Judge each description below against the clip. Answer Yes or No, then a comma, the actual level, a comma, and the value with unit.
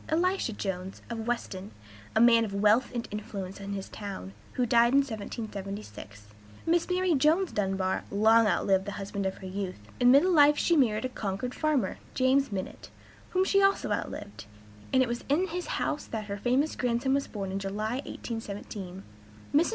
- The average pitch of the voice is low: No, high, 225 Hz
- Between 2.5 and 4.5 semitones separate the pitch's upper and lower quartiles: No, wide, 5.6 semitones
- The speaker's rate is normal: Yes, average, 175 wpm